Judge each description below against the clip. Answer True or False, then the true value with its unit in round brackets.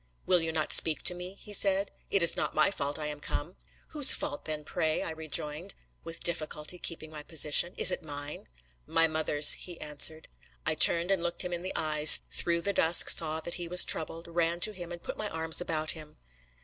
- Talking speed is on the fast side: True (215 wpm)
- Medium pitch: True (165 Hz)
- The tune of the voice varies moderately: False (2.3 semitones)